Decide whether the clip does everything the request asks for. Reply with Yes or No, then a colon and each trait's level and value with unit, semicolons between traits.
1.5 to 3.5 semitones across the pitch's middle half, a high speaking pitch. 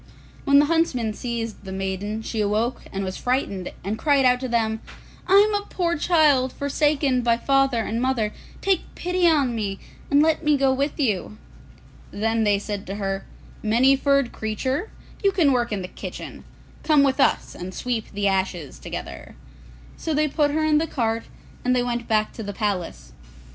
No: wide, 5.4 semitones; high, 245 Hz